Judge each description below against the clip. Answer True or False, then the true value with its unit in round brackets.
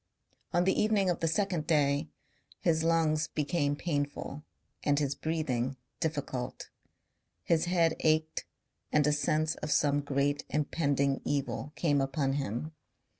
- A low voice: False (150 Hz)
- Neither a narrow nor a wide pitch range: False (2.3 semitones)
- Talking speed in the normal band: False (130 wpm)